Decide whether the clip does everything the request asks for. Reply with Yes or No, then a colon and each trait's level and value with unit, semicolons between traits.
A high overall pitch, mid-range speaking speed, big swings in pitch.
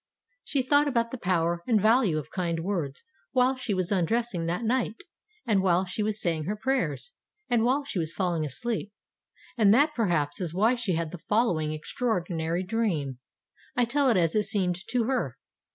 Yes: high, 200 Hz; average, 185 wpm; wide, 5.9 semitones